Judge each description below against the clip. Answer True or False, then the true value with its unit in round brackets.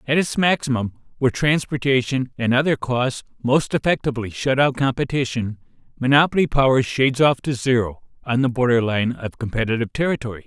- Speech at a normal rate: True (150 wpm)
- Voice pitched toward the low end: True (130 Hz)